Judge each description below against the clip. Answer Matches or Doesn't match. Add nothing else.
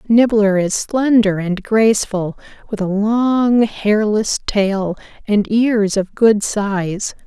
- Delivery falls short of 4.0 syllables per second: Matches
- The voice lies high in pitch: Matches